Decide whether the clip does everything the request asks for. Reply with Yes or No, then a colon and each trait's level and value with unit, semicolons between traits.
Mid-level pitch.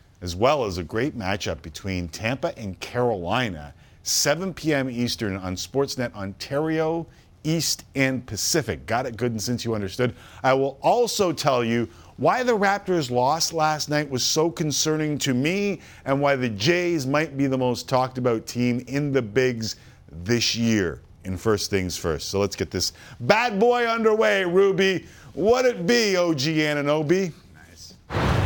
No: low, 130 Hz